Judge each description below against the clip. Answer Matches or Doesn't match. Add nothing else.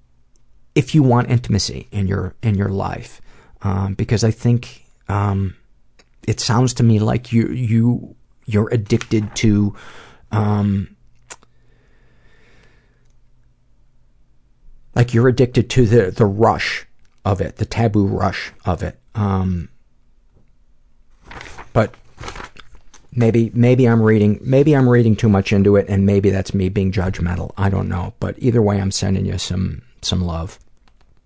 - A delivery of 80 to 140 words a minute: Matches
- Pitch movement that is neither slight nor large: Matches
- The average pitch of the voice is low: Matches